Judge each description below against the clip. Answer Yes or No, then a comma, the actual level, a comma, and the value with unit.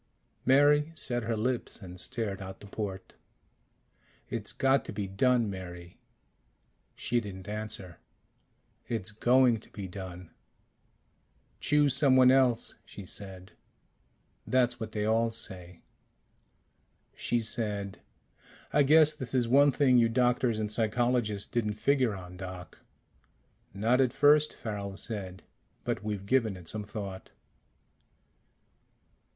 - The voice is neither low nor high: No, low, 110 Hz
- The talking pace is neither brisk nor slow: No, slow, 125 wpm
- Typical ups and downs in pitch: Yes, average, 4.4 semitones